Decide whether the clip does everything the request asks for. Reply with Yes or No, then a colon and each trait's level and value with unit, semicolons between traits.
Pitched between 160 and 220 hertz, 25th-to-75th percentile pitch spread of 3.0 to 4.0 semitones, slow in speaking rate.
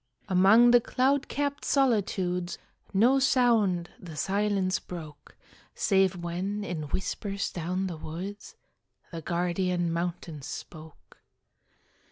Yes: medium, 185 Hz; average, 3.3 semitones; slow, 105 wpm